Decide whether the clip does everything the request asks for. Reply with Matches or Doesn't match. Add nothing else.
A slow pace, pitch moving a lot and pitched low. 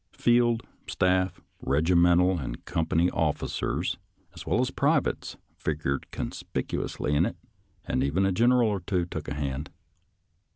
Doesn't match